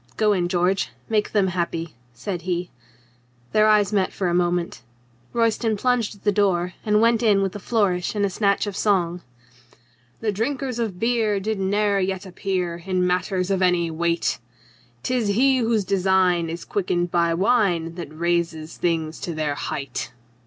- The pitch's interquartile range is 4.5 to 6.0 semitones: No, average, 3.3 semitones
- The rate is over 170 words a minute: No, average, 165 wpm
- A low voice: No, high, 190 Hz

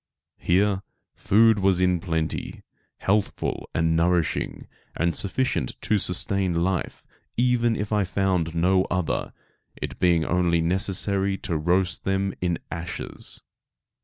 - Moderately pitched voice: No, very low, 90 Hz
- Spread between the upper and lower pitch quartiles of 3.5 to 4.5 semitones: No, narrow, 2.6 semitones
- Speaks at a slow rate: Yes, slow, 120 wpm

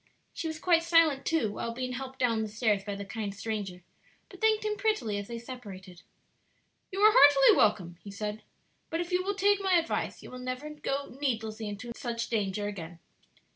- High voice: Yes, high, 240 Hz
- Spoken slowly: No, average, 195 wpm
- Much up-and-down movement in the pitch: Yes, wide, 7.8 semitones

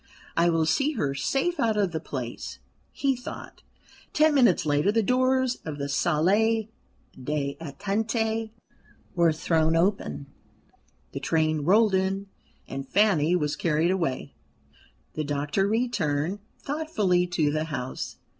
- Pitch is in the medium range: Yes, medium, 180 Hz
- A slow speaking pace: Yes, slow, 125 wpm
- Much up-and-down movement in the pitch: Yes, wide, 6.5 semitones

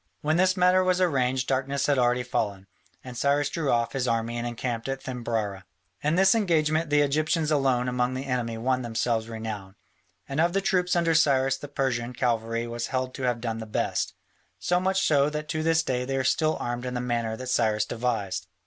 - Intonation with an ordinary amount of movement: Yes, average, 4.4 semitones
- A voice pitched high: No, low, 130 Hz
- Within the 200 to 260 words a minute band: Yes, fast, 205 wpm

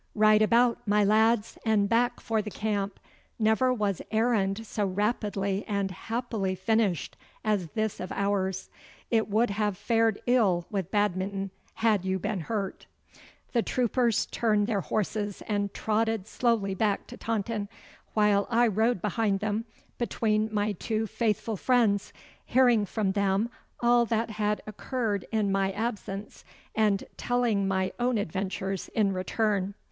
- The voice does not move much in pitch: Yes, narrow, 2.3 semitones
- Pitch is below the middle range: No, high, 210 Hz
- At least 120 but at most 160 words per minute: Yes, average, 140 wpm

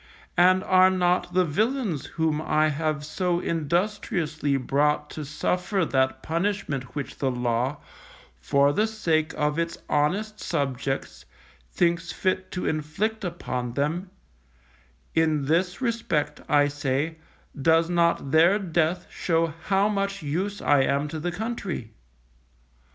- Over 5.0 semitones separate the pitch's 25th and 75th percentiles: No, average, 4.1 semitones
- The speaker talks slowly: Yes, slow, 130 wpm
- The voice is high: No, medium, 160 Hz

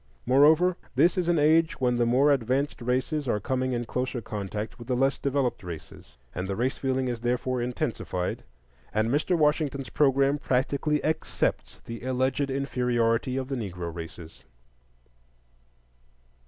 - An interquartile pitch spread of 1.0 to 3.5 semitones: Yes, average, 3.1 semitones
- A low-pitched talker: Yes, low, 130 Hz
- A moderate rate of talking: Yes, average, 145 wpm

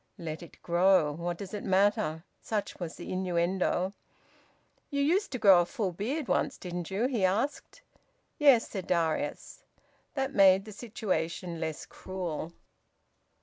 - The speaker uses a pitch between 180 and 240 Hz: Yes, high, 190 Hz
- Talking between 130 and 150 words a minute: Yes, average, 145 wpm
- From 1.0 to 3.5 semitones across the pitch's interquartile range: No, average, 4.0 semitones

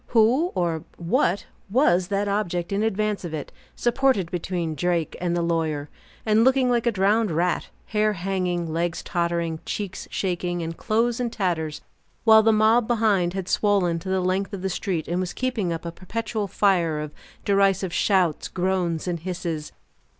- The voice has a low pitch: No, medium, 185 Hz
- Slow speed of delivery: No, average, 170 wpm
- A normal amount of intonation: Yes, average, 3.8 semitones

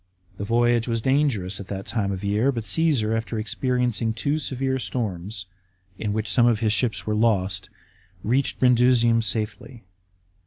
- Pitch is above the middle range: No, low, 115 Hz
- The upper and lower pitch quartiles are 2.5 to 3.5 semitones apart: Yes, average, 3.0 semitones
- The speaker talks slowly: No, average, 160 wpm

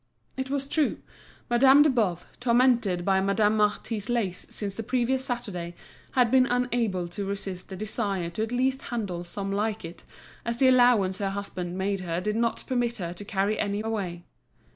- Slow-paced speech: No, average, 180 wpm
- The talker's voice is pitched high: Yes, high, 210 Hz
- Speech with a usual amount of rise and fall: Yes, average, 4.2 semitones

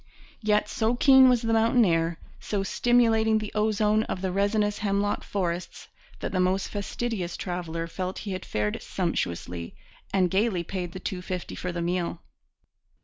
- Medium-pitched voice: No, high, 195 Hz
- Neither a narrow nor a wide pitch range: Yes, average, 3.5 semitones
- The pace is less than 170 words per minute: Yes, average, 160 wpm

